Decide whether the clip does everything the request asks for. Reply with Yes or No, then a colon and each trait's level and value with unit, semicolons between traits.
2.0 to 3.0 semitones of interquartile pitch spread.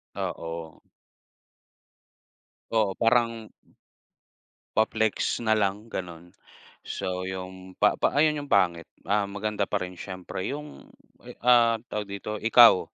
No: average, 3.7 semitones